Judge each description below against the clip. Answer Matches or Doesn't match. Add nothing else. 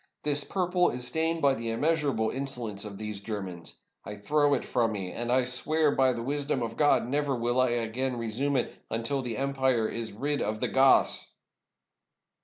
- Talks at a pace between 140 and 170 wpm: Doesn't match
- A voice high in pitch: Doesn't match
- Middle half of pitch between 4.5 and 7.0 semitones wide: Doesn't match